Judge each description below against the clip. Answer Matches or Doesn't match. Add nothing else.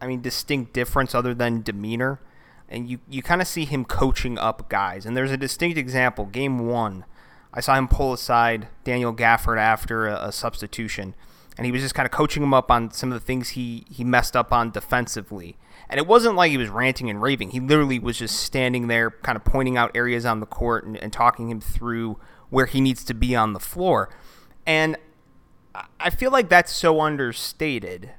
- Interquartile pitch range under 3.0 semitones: Matches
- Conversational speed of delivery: Doesn't match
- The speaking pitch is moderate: Doesn't match